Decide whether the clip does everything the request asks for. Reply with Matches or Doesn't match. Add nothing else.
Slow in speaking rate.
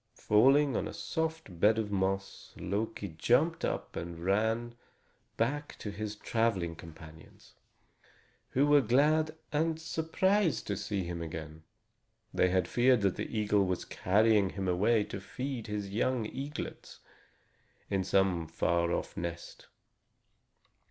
Matches